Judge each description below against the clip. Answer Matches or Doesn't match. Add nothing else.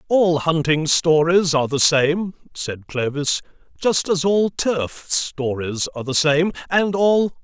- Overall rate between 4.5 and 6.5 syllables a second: Doesn't match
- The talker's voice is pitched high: Doesn't match